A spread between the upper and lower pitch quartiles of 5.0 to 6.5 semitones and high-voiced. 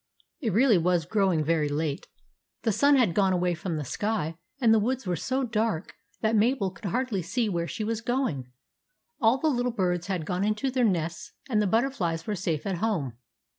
Yes: average, 5.3 semitones; high, 200 Hz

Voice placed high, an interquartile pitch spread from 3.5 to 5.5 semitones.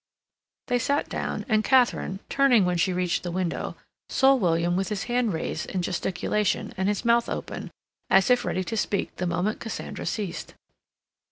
Yes: high, 195 Hz; average, 4.8 semitones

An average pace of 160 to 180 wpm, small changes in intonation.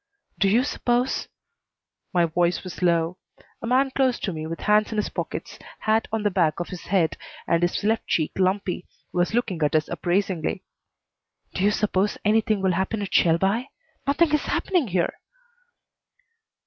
No: average, 170 wpm; average, 4.1 semitones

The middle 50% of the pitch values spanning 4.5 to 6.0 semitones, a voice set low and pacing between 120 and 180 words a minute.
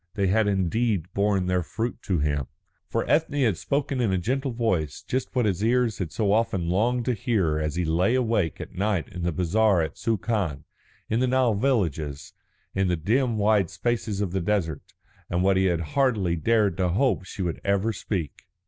No: average, 4.8 semitones; low, 100 Hz; average, 195 wpm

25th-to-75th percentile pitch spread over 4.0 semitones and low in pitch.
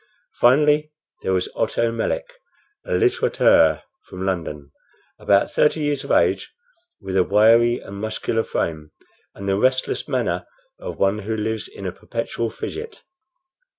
Yes: average, 4.9 semitones; low, 110 Hz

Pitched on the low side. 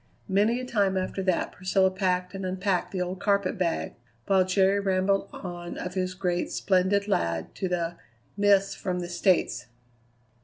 No: medium, 185 Hz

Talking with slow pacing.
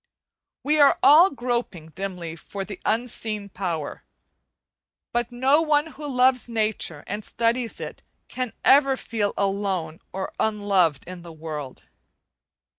Yes: slow, 125 wpm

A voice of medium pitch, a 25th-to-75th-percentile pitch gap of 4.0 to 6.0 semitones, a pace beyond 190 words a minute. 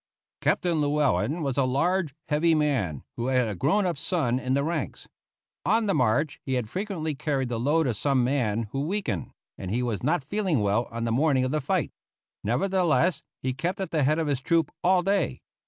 Yes: medium, 145 Hz; average, 5.2 semitones; fast, 205 wpm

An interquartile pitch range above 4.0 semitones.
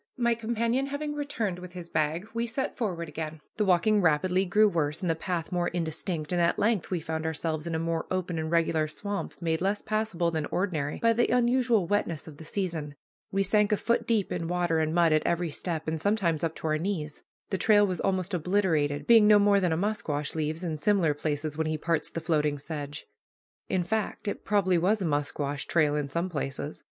Yes: average, 4.5 semitones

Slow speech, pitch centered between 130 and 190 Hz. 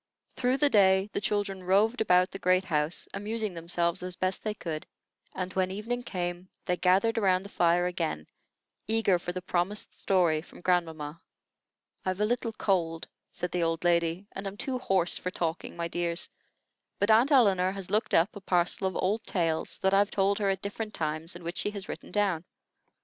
No: average, 190 wpm; medium, 185 Hz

